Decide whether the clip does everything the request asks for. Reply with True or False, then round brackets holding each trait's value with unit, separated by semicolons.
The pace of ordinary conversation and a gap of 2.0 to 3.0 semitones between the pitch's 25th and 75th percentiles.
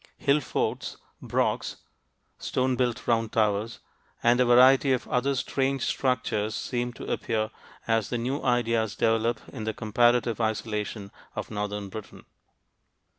False (130 wpm; 2.5 semitones)